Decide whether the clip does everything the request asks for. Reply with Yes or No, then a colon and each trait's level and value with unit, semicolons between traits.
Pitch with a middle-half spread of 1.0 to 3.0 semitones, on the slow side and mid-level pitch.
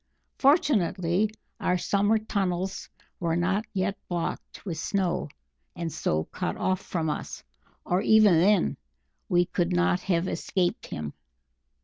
Yes: average, 2.7 semitones; slow, 125 wpm; medium, 180 Hz